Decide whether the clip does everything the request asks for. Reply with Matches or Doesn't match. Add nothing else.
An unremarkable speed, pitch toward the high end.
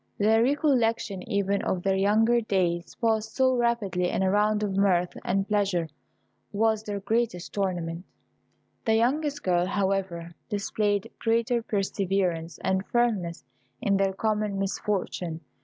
Doesn't match